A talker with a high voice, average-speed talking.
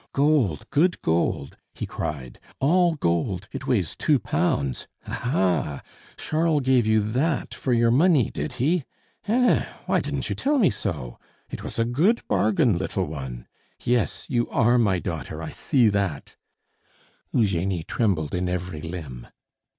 No: low, 110 Hz; average, 150 wpm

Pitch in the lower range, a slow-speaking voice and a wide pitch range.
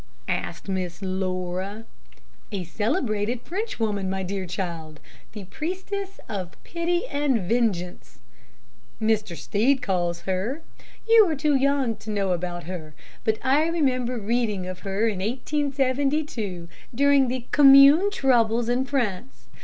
No: high, 225 Hz; slow, 125 wpm; wide, 6.7 semitones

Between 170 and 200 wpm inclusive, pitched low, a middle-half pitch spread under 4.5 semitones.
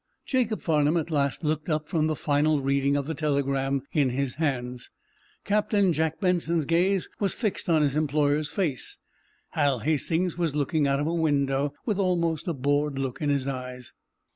No: average, 175 wpm; medium, 150 Hz; average, 3.2 semitones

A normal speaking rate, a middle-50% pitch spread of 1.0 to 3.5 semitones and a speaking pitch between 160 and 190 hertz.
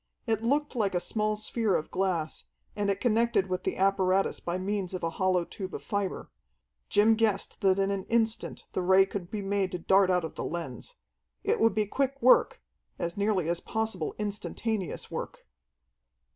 No: average, 185 wpm; average, 3.0 semitones; high, 200 Hz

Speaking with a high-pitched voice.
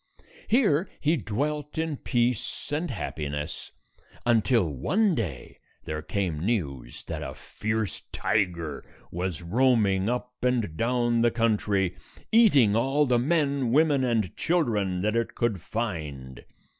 No: low, 115 Hz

